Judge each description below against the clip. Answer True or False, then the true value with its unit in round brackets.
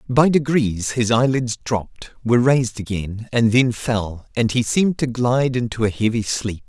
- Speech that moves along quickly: False (180 wpm)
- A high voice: False (120 Hz)